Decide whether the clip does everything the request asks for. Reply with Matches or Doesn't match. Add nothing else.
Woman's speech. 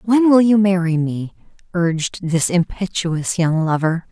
Matches